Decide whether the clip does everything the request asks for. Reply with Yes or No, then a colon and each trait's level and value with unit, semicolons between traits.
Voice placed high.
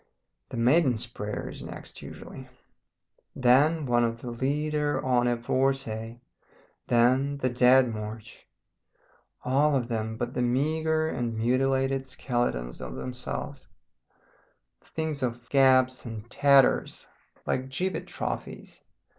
No: low, 125 Hz